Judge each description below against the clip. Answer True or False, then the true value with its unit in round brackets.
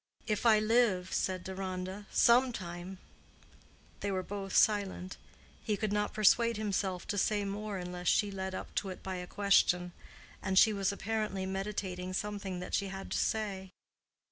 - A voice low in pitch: False (195 Hz)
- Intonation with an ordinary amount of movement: False (2.0 semitones)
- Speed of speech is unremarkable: True (160 wpm)